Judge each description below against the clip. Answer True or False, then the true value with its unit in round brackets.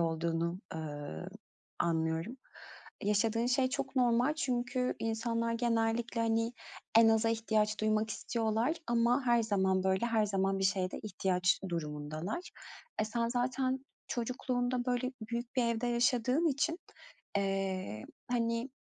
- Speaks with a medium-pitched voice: False (230 Hz)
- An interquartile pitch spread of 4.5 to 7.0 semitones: False (4.1 semitones)